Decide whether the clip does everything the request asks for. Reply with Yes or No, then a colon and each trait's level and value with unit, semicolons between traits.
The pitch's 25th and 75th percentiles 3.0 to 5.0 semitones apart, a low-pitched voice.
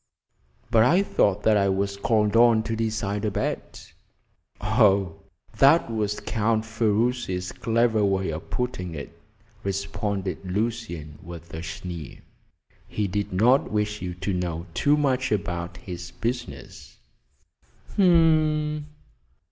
Yes: average, 4.3 semitones; low, 105 Hz